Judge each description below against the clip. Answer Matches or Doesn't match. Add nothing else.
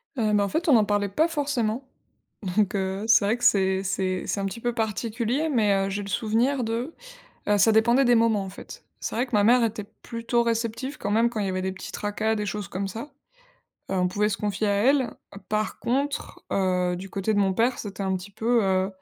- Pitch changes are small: Doesn't match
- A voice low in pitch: Doesn't match